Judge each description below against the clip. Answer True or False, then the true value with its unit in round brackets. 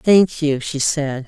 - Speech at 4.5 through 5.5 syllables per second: False (3.3 syllables/s)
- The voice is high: False (150 Hz)